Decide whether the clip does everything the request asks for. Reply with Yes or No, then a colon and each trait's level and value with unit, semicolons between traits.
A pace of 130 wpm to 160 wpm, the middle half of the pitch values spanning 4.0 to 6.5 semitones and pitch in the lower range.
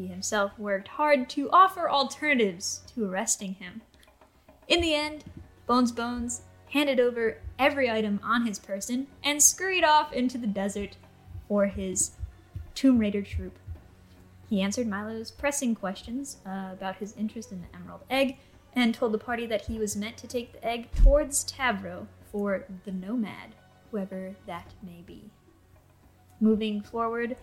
No: average, 150 wpm; average, 4.7 semitones; high, 215 Hz